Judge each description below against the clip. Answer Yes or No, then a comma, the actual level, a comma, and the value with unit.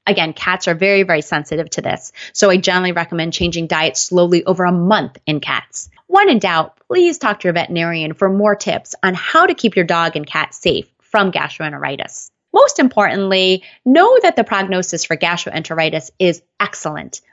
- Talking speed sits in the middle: Yes, average, 180 wpm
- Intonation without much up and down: No, average, 3.6 semitones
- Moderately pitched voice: Yes, medium, 180 Hz